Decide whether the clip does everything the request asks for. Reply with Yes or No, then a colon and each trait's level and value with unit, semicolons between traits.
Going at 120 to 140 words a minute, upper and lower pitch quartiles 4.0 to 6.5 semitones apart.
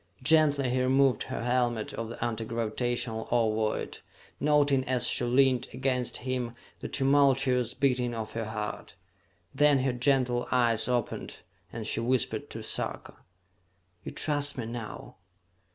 No: slow, 135 wpm; narrow, 2.5 semitones